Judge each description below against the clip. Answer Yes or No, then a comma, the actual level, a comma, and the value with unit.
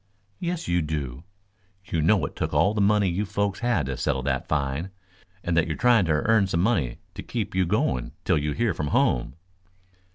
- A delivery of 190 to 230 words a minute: Yes, fast, 205 wpm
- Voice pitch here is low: Yes, very low, 85 Hz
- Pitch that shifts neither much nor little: No, wide, 6.0 semitones